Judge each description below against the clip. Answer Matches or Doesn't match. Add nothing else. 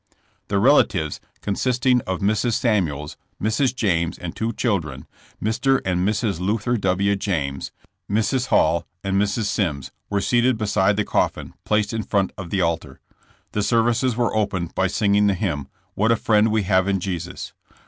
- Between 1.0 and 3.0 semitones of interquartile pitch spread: Doesn't match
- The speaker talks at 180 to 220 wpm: Doesn't match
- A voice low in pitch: Matches